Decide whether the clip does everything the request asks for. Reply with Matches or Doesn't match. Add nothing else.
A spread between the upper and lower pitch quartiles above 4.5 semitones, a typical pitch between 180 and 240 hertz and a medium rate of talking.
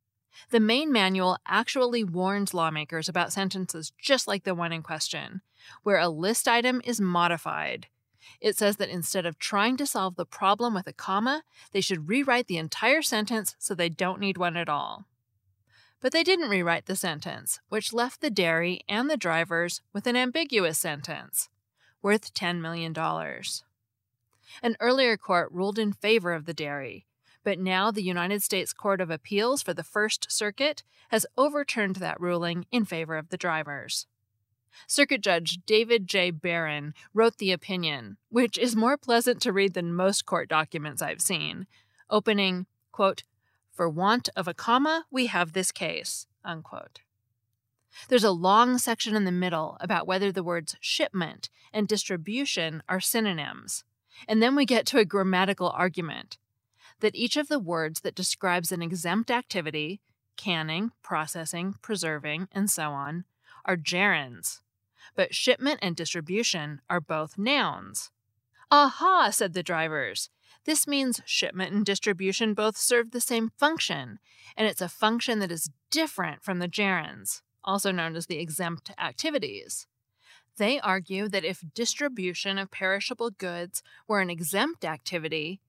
Matches